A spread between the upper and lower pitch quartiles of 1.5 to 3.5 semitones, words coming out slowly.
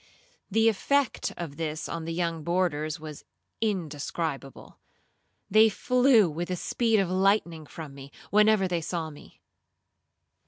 No: average, 5.1 semitones; slow, 130 wpm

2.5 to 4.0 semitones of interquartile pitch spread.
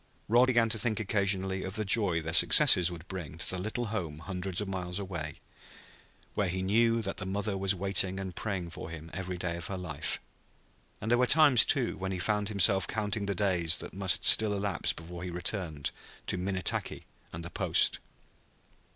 Yes: average, 2.9 semitones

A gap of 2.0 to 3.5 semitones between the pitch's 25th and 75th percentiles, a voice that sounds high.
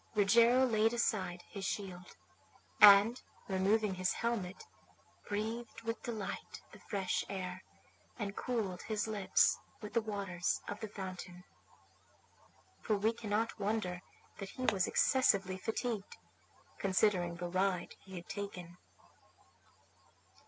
Yes: average, 3.0 semitones; high, 200 Hz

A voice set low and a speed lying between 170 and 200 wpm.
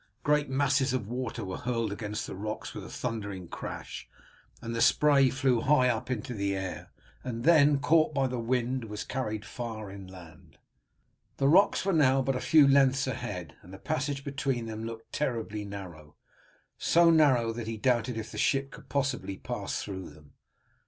Yes: low, 120 Hz; average, 180 wpm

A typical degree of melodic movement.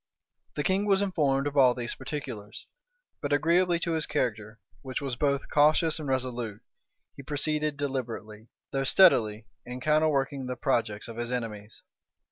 Yes: average, 4.2 semitones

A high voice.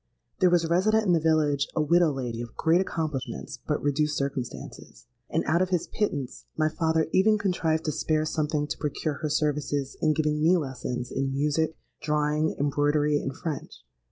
No: medium, 155 Hz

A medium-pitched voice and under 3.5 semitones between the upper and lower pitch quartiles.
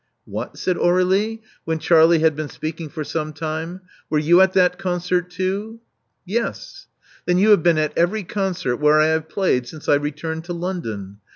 Yes: medium, 170 Hz; average, 3.1 semitones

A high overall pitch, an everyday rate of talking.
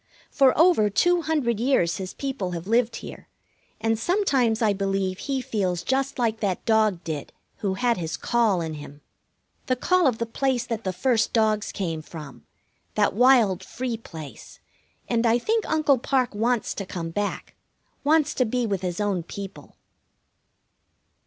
Yes: high, 225 Hz; average, 165 wpm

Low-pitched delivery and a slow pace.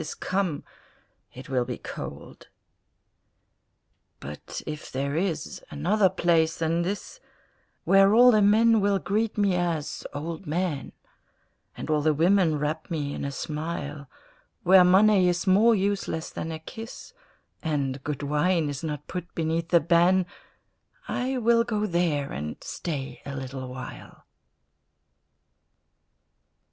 No: medium, 170 Hz; slow, 130 wpm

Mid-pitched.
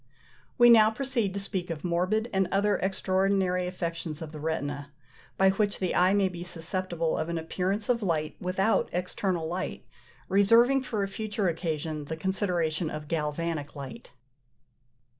Yes: medium, 180 Hz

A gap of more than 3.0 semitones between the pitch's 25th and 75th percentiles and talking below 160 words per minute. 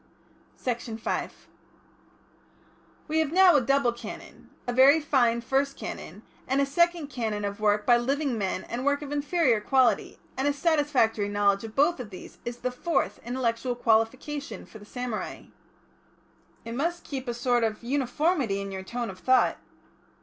No: average, 4.1 semitones; average, 165 wpm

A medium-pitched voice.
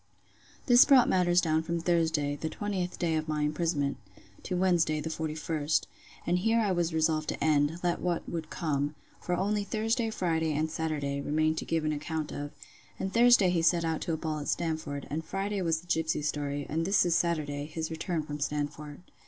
Yes: medium, 160 Hz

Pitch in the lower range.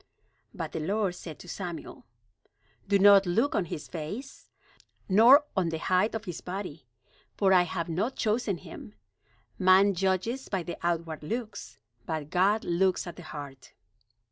No: medium, 185 Hz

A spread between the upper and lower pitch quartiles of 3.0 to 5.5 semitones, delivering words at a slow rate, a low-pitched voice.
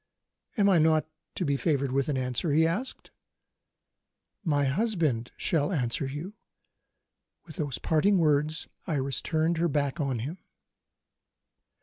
No: average, 3.4 semitones; slow, 130 wpm; medium, 155 Hz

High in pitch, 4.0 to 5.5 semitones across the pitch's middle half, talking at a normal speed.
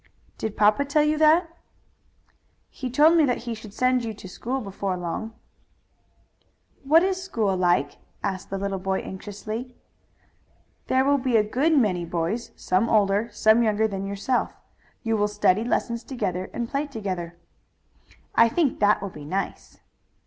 Yes: high, 220 Hz; average, 4.7 semitones; average, 160 wpm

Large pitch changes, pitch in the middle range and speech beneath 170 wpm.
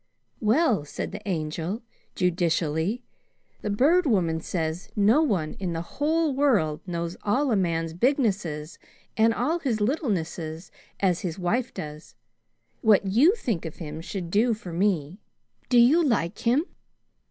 No: wide, 6.7 semitones; high, 195 Hz; average, 140 wpm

